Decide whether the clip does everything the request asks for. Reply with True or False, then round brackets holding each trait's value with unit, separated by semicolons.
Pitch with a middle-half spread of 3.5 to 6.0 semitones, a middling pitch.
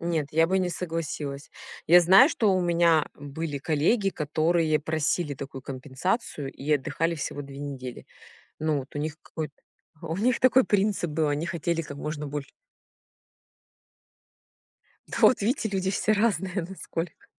True (4.0 semitones; 160 Hz)